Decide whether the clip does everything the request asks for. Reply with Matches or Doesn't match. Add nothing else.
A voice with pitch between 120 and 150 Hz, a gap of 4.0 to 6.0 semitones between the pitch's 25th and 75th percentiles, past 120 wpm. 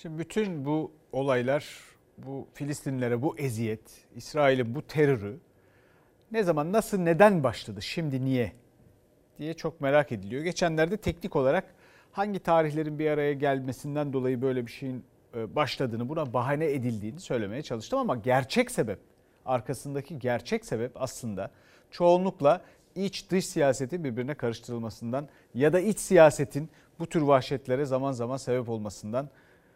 Matches